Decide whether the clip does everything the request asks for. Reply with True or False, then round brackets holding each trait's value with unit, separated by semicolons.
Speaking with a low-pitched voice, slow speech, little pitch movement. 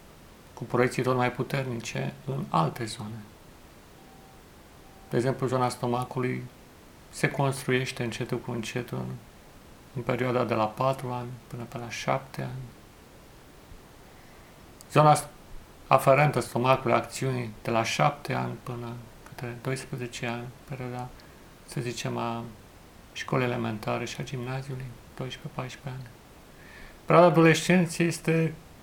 True (125 Hz; 110 wpm; 2.1 semitones)